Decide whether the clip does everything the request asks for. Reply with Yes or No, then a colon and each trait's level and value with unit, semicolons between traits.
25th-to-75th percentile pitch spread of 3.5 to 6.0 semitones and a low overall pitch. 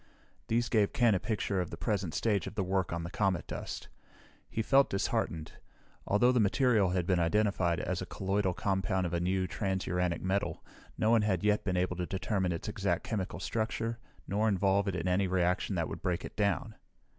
No: average, 2.7 semitones; very low, 95 Hz